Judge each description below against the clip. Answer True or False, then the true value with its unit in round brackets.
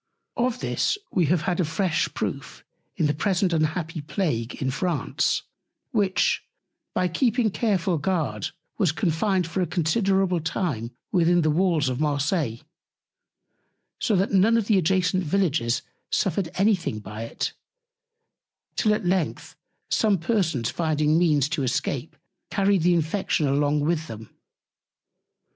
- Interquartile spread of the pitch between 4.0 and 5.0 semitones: True (4.3 semitones)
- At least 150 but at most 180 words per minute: False (135 wpm)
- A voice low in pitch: False (170 Hz)